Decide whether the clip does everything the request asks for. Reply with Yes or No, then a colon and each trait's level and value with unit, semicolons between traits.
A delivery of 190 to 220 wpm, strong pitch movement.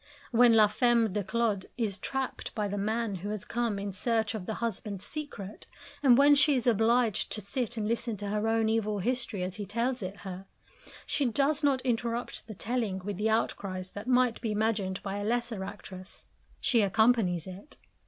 No: average, 195 wpm; average, 3.1 semitones